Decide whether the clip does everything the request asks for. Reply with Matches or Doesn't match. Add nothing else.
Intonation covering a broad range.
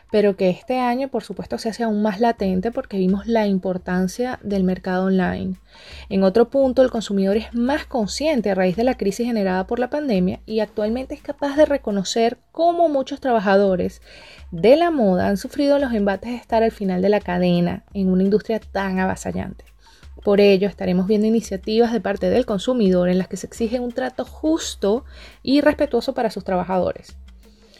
Doesn't match